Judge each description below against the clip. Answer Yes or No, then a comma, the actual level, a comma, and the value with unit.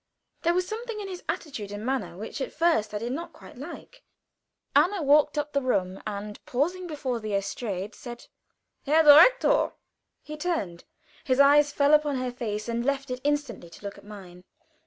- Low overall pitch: No, very high, 270 Hz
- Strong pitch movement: Yes, wide, 6.3 semitones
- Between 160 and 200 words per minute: Yes, average, 180 wpm